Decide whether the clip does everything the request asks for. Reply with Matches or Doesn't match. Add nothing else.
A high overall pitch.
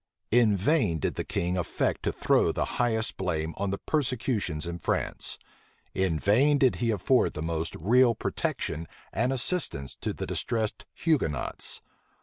Doesn't match